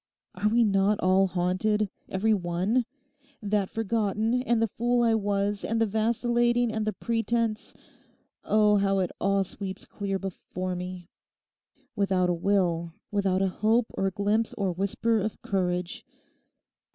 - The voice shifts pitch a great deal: No, average, 2.9 semitones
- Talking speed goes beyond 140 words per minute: No, slow, 135 wpm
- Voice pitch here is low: No, high, 200 Hz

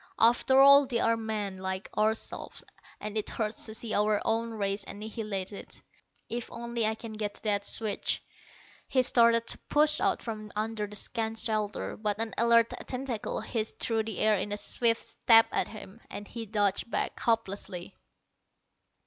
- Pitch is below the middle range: No, high, 220 Hz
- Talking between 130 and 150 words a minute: No, average, 165 wpm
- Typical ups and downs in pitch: No, narrow, 1.9 semitones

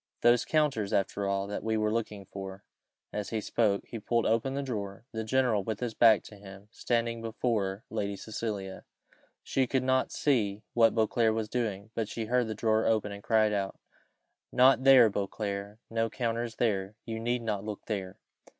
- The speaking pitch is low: Yes, low, 110 Hz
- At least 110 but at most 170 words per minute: No, average, 185 wpm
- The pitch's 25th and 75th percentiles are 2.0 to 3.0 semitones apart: Yes, narrow, 2.6 semitones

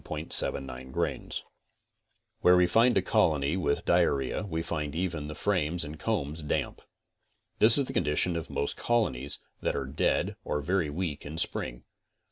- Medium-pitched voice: No, very low, 80 Hz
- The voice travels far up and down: No, average, 3.8 semitones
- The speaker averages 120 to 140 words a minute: No, average, 165 wpm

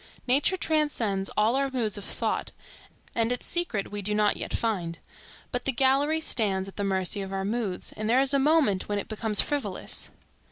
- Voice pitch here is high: Yes, high, 220 Hz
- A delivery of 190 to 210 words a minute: Yes, average, 195 wpm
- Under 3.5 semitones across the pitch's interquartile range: No, average, 5.1 semitones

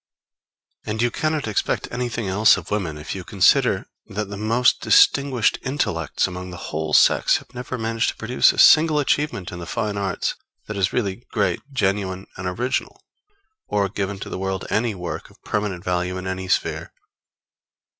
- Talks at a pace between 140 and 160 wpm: No, average, 175 wpm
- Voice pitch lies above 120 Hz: No, low, 100 Hz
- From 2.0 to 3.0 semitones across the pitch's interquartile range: No, average, 4.3 semitones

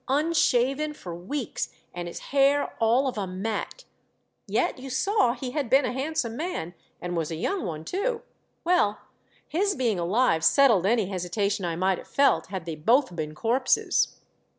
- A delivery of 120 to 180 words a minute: Yes, average, 175 wpm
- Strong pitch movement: Yes, wide, 7.6 semitones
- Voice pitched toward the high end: Yes, high, 235 Hz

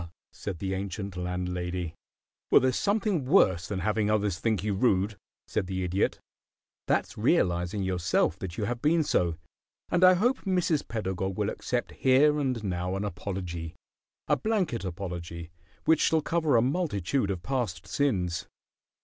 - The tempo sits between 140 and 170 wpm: Yes, average, 150 wpm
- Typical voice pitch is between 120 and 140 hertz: No, low, 100 Hz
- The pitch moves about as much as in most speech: No, wide, 6.7 semitones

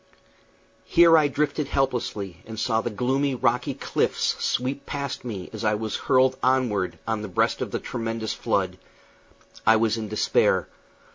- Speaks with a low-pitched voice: Yes, low, 115 Hz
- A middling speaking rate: Yes, average, 155 wpm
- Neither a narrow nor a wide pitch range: Yes, average, 3.6 semitones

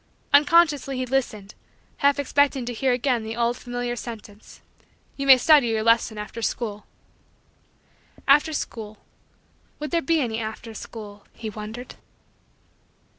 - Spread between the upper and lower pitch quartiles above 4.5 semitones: No, average, 3.9 semitones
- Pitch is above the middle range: Yes, high, 245 Hz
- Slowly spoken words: Yes, slow, 130 wpm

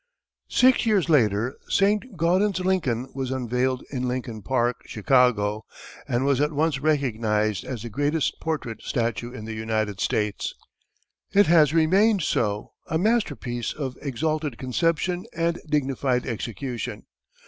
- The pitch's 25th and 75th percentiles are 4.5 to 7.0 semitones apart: Yes, wide, 5.5 semitones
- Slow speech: Yes, slow, 130 wpm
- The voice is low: Yes, low, 130 Hz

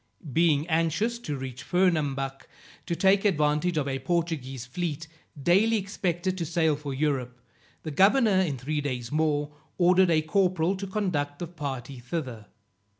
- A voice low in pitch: No, medium, 160 Hz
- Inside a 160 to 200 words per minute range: No, average, 150 wpm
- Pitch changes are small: No, average, 4.5 semitones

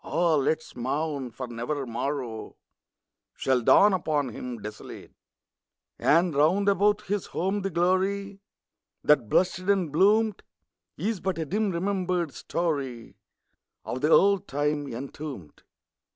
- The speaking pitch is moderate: Yes, medium, 160 Hz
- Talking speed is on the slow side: Yes, slow, 130 wpm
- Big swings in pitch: Yes, wide, 6.1 semitones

